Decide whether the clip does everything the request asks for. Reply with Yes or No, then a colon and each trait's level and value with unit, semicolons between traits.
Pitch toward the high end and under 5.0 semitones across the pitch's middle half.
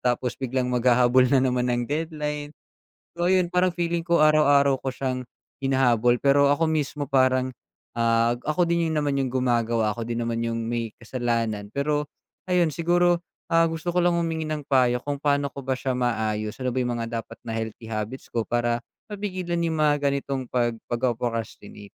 No: low, 130 Hz; average, 4.4 semitones